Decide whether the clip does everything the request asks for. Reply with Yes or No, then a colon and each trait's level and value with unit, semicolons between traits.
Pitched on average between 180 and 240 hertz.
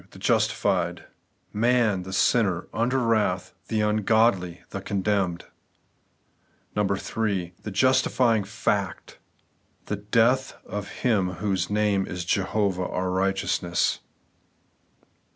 No: low, 100 Hz